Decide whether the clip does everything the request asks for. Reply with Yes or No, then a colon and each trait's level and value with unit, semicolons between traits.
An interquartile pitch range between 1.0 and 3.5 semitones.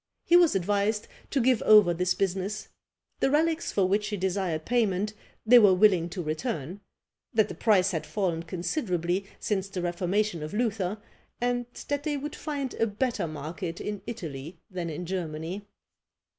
No: average, 4.2 semitones